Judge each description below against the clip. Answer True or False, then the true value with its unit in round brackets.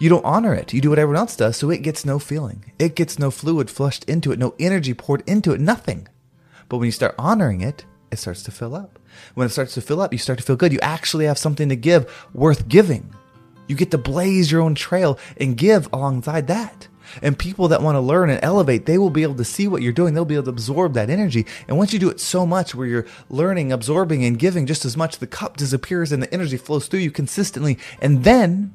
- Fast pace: True (255 wpm)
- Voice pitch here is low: False (150 Hz)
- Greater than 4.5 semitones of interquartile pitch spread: True (5.2 semitones)